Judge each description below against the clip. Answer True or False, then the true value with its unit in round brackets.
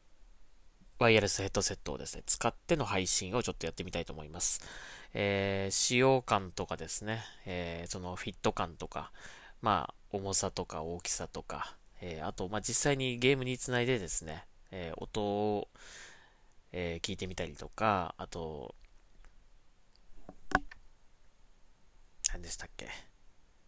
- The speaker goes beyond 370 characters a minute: False (280 characters per minute)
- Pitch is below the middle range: True (95 Hz)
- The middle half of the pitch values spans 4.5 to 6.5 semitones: False (3.4 semitones)